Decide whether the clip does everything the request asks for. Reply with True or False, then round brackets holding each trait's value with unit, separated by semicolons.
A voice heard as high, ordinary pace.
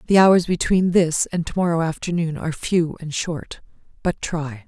False (165 Hz; 180 wpm)